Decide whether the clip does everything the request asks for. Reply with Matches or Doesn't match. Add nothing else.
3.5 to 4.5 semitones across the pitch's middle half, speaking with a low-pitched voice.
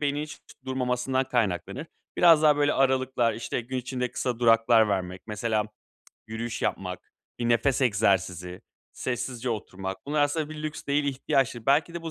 Matches